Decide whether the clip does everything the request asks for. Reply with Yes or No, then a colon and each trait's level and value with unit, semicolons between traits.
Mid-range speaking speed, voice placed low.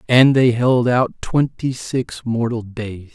Yes: average, 155 wpm; low, 120 Hz